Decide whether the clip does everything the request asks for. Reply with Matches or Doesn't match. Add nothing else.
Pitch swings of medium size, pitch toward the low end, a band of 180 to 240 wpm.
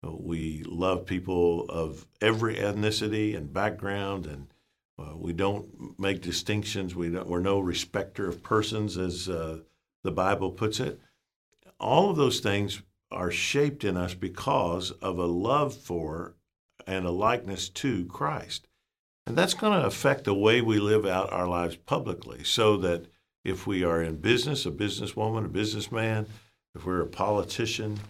Doesn't match